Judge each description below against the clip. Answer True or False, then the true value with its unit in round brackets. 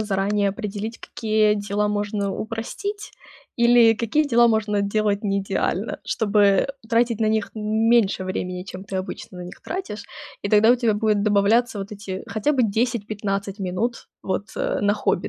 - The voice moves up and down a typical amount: False (2.2 semitones)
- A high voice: True (210 Hz)